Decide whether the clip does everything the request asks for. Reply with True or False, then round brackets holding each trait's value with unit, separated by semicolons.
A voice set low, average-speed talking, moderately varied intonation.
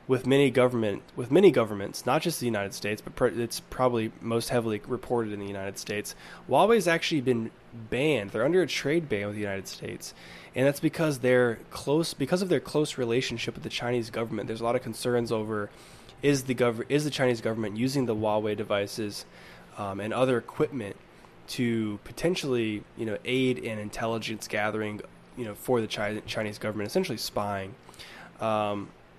True (115 Hz; 180 wpm; 3.2 semitones)